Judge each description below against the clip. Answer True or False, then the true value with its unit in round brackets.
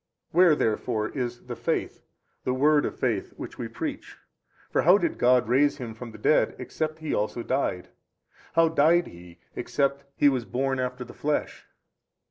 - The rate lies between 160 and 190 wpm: True (170 wpm)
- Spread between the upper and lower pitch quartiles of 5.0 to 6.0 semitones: False (4.0 semitones)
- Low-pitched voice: True (130 Hz)